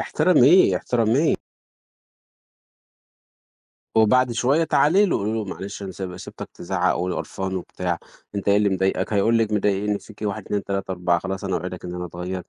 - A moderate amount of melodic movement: Yes, average, 3.3 semitones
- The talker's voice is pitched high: No, low, 100 Hz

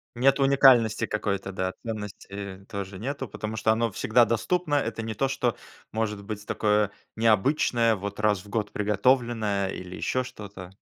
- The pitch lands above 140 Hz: No, low, 110 Hz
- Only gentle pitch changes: No, average, 3.0 semitones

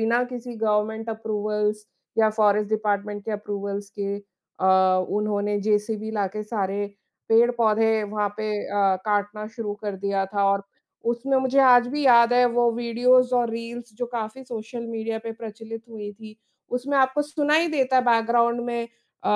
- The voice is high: Yes, high, 220 Hz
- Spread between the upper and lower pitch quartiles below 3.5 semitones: Yes, narrow, 2.4 semitones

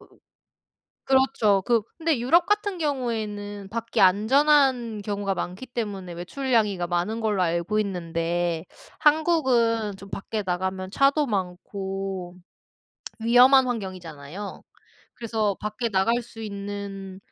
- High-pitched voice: Yes, high, 210 Hz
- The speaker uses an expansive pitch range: No, average, 4.3 semitones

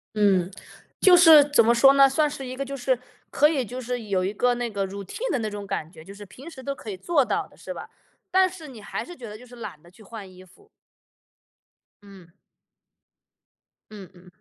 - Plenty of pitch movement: Yes, wide, 5.8 semitones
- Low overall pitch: No, high, 235 Hz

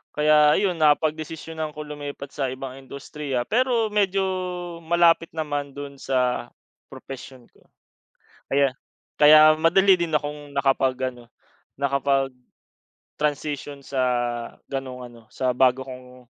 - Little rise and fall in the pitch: No, average, 3.1 semitones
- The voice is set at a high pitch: No, medium, 140 Hz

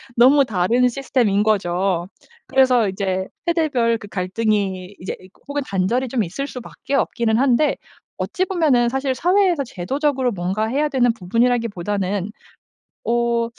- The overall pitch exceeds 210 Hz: Yes, high, 235 Hz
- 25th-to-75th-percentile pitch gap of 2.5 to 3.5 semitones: No, average, 5.1 semitones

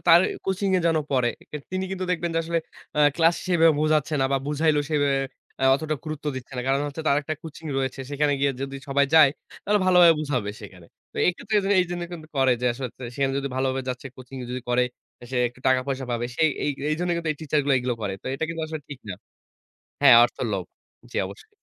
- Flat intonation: No, average, 3.8 semitones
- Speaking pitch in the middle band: Yes, medium, 145 Hz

